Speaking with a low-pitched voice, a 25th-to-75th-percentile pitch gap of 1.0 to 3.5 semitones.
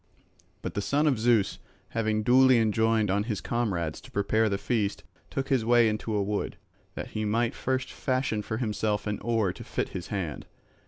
Yes: low, 110 Hz; narrow, 2.6 semitones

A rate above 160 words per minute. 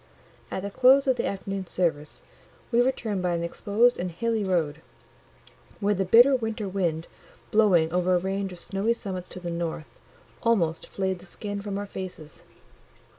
Yes: average, 170 wpm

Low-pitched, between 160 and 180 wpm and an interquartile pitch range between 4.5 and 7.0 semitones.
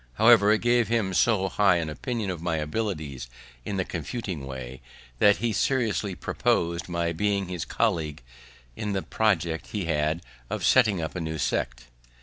Yes: very low, 90 Hz; average, 165 wpm; average, 5.0 semitones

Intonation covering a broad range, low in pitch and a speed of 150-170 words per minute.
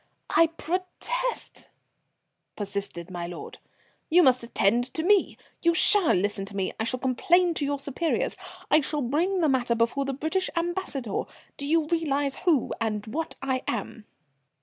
No: wide, 6.4 semitones; very high, 275 Hz; average, 155 wpm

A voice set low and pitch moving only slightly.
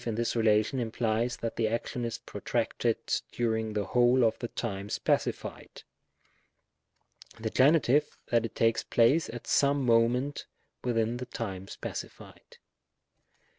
Yes: low, 115 Hz; narrow, 1.9 semitones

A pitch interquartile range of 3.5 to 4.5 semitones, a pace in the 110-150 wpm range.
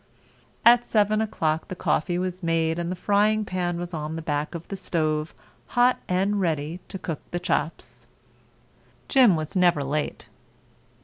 No: average, 3.8 semitones; average, 160 wpm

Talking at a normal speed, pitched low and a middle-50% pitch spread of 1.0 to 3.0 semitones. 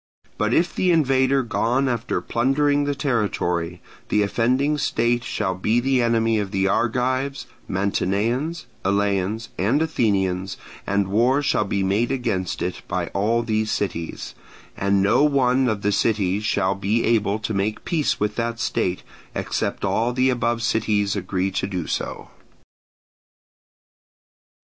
No: average, 145 wpm; low, 110 Hz; average, 4.3 semitones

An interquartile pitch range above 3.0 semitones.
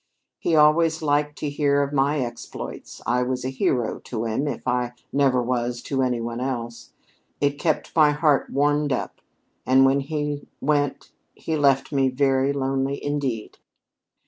No: narrow, 2.5 semitones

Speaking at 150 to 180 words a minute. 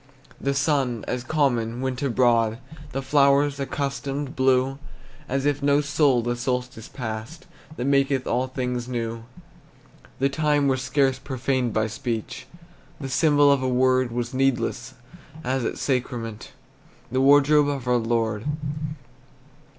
No: slow, 135 wpm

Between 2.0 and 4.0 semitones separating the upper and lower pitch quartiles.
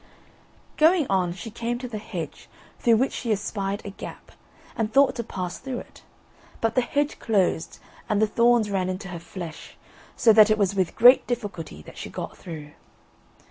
No: average, 4.4 semitones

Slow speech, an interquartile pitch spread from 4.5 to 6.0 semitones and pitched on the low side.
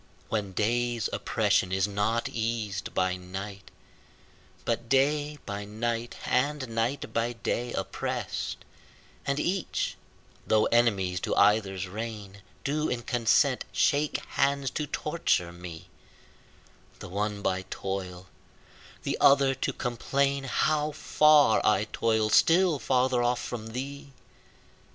Yes: slow, 120 wpm; average, 5.3 semitones; low, 115 Hz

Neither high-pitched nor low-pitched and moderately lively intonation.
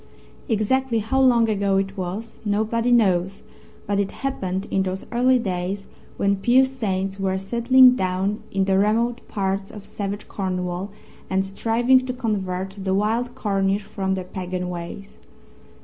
No: high, 200 Hz; average, 3.3 semitones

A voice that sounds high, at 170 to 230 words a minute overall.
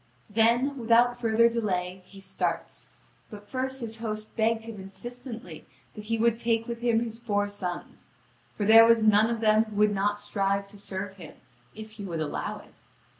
Yes: high, 220 Hz; average, 180 wpm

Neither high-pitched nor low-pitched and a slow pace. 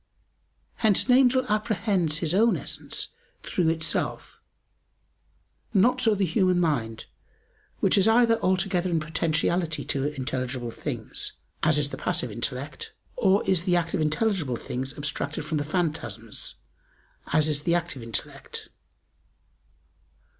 Yes: medium, 165 Hz; slow, 130 wpm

